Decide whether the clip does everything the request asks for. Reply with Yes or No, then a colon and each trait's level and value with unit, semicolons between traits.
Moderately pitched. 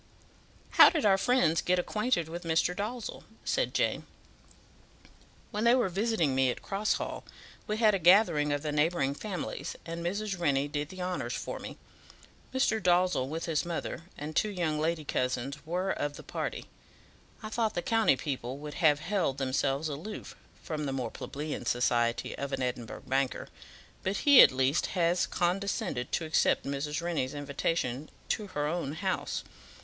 Yes: medium, 165 Hz